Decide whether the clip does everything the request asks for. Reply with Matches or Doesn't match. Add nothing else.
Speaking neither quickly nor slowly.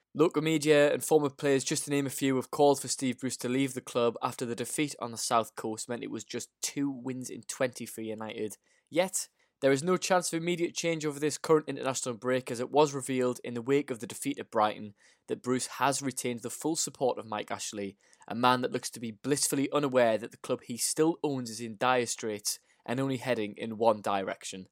Doesn't match